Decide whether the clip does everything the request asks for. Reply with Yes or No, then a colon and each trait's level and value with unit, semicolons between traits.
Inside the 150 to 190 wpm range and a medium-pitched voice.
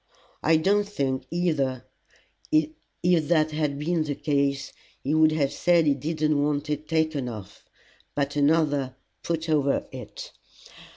No: slow, 135 wpm; medium, 150 Hz